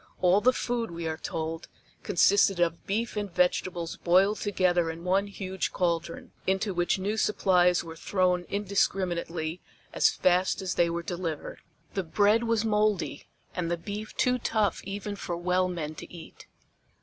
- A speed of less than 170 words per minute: Yes, average, 160 wpm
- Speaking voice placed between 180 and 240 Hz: Yes, medium, 185 Hz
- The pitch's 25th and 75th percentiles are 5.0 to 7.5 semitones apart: No, average, 2.9 semitones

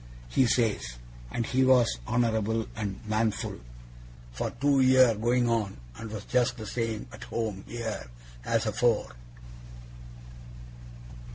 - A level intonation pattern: Yes, narrow, 2.2 semitones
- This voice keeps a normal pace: No, slow, 125 wpm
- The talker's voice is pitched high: No, low, 115 Hz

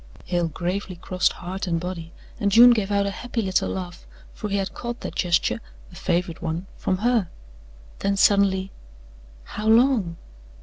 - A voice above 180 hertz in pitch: Yes, high, 190 Hz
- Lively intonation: No, average, 3.0 semitones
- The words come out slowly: No, average, 165 wpm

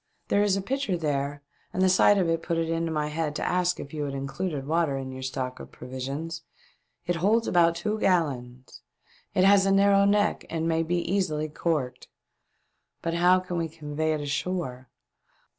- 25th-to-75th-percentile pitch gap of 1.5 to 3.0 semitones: No, average, 4.2 semitones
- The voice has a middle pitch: Yes, medium, 165 Hz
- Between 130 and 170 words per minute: No, average, 190 wpm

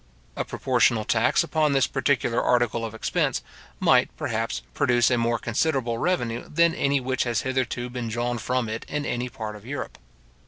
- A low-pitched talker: Yes, low, 120 Hz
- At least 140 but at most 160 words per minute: No, average, 170 wpm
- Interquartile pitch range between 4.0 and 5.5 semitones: No, narrow, 2.6 semitones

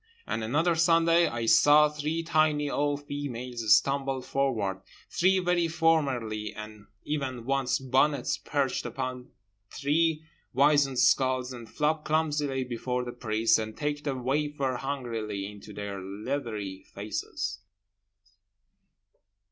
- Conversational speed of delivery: No, slow, 115 wpm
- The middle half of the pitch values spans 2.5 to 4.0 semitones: No, average, 4.5 semitones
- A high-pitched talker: No, low, 135 Hz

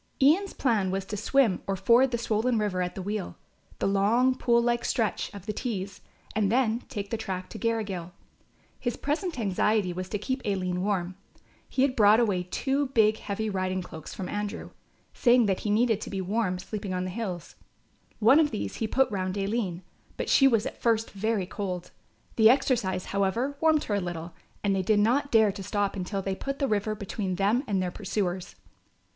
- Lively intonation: No, average, 3.8 semitones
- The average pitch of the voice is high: Yes, high, 210 Hz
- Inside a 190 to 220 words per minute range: Yes, average, 200 wpm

